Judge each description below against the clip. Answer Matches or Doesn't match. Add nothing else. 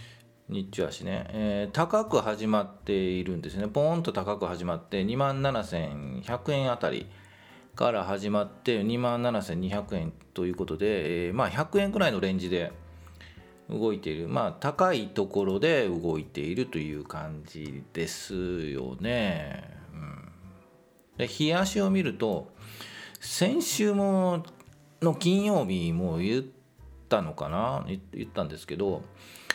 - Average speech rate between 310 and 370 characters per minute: Doesn't match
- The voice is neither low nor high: Doesn't match